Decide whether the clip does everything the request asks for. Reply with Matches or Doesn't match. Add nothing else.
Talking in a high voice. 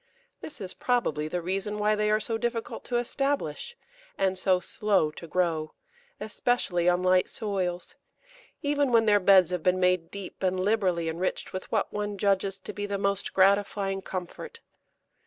Matches